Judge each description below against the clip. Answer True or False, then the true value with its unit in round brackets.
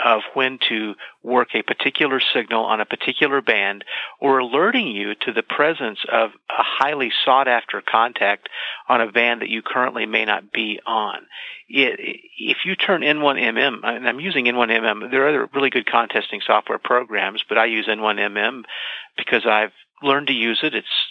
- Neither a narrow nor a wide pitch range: False (8.8 semitones)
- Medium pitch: False (130 Hz)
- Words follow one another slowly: False (170 wpm)